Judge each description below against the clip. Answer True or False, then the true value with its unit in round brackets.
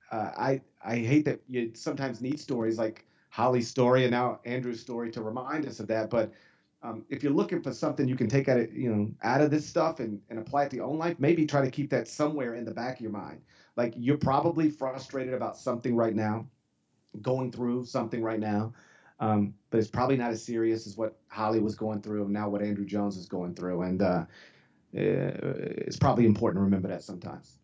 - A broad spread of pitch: False (3.5 semitones)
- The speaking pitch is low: True (120 Hz)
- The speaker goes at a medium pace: False (220 wpm)